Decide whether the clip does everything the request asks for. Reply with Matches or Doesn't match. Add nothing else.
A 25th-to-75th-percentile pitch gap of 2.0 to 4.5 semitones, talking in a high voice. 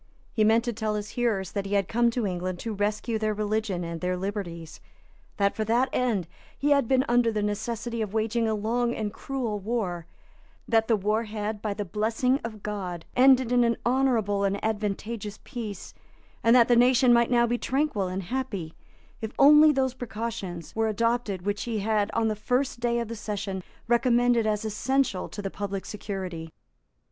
Matches